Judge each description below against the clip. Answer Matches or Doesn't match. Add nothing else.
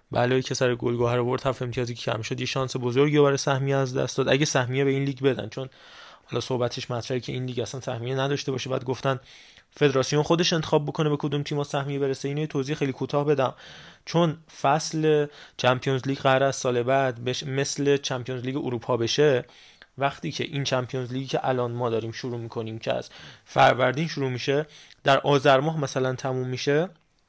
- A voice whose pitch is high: Doesn't match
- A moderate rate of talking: Doesn't match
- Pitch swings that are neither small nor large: Doesn't match